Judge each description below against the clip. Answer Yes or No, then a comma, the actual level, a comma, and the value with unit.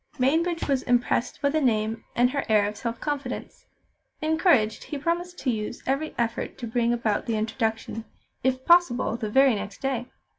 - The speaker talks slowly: No, average, 175 wpm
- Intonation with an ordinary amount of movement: Yes, average, 4.2 semitones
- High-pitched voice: Yes, high, 245 Hz